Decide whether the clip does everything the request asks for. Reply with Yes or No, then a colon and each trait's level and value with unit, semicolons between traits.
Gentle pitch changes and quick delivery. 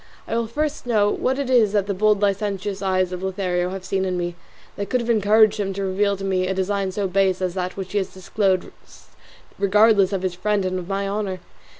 Yes: narrow, 1.9 semitones; fast, 230 wpm